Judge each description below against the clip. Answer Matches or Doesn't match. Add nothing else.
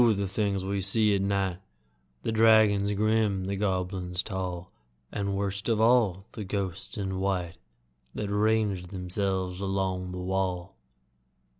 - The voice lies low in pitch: Matches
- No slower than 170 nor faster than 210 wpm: Doesn't match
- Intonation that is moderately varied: Doesn't match